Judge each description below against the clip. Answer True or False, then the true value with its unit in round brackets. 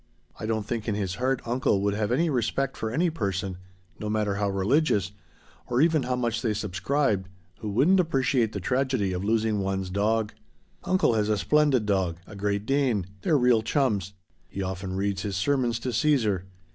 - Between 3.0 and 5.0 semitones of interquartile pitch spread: True (4.6 semitones)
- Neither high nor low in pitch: False (110 Hz)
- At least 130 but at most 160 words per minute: False (185 wpm)